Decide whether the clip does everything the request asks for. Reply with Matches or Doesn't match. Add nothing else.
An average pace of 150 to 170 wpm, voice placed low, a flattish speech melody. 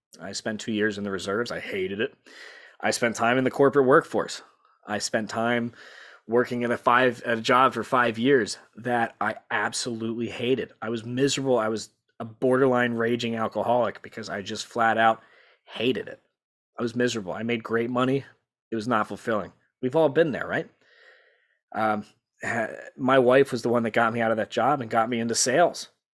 Doesn't match